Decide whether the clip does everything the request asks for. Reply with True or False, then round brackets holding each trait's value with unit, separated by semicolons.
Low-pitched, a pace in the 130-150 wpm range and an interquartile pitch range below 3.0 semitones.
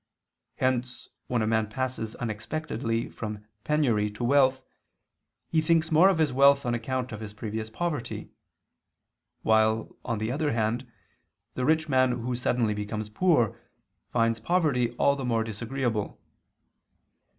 False (120 Hz; 140 wpm; 3.9 semitones)